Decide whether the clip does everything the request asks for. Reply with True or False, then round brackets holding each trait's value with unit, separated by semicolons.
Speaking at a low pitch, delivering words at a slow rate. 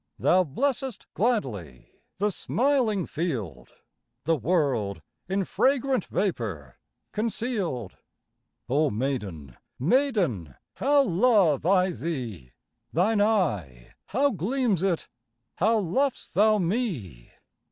False (180 Hz; 95 wpm)